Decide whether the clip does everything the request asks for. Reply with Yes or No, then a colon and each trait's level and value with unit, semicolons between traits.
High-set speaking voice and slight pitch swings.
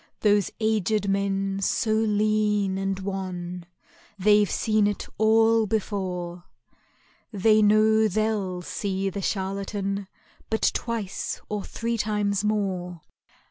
Yes: high, 205 Hz; narrow, 1.9 semitones